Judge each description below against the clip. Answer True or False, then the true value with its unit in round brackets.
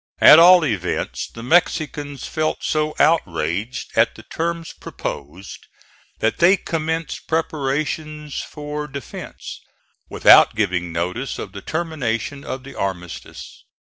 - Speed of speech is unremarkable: False (115 wpm)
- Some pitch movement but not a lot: False (6.5 semitones)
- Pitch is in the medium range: True (145 Hz)